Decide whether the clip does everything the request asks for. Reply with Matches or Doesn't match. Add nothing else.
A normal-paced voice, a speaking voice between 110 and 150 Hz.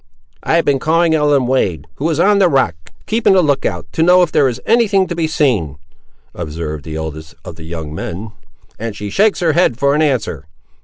Doesn't match